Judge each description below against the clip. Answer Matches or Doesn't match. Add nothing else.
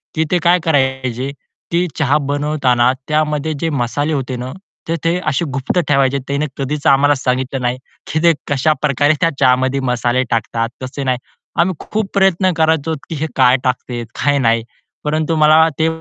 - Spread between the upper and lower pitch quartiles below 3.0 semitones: Doesn't match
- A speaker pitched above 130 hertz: Matches